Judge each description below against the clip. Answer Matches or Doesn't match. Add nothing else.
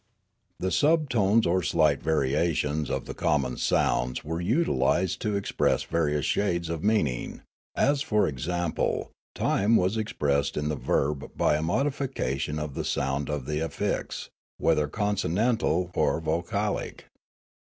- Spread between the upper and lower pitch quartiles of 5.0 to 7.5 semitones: Matches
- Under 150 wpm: Matches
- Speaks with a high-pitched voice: Doesn't match